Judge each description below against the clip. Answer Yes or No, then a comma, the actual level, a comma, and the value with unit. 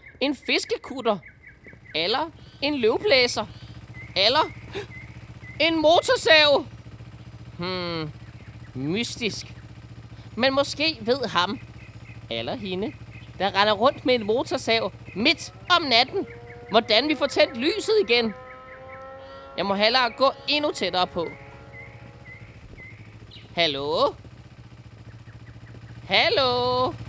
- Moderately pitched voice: Yes, medium, 175 Hz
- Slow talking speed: Yes, slow, 90 wpm